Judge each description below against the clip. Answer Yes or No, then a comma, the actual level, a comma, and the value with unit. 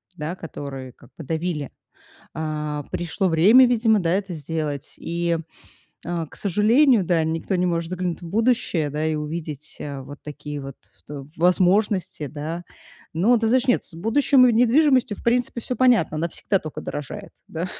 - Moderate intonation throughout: No, wide, 6.1 semitones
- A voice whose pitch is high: No, medium, 170 Hz